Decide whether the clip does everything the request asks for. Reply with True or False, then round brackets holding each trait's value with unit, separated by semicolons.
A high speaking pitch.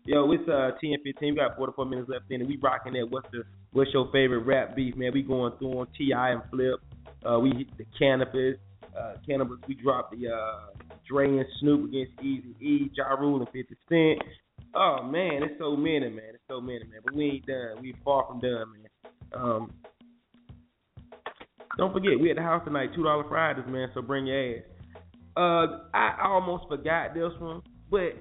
False (135 Hz)